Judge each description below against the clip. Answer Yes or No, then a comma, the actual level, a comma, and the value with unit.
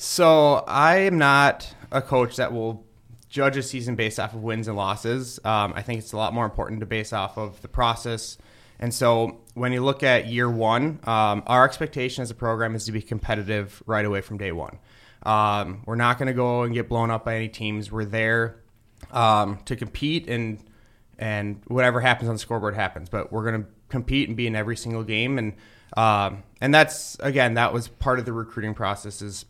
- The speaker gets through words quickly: Yes, fast, 210 wpm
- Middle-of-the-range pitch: No, low, 115 Hz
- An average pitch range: No, narrow, 2.3 semitones